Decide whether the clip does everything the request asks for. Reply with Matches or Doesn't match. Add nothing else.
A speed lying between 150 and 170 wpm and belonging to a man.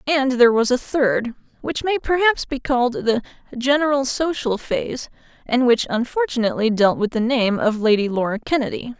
Doesn't match